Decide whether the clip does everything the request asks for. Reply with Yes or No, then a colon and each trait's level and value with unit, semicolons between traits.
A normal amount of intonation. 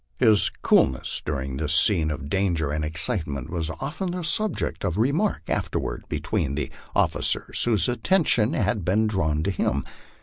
No: wide, 7.1 semitones